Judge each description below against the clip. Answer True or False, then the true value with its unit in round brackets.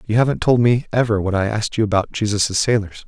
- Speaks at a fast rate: True (235 wpm)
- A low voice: True (110 Hz)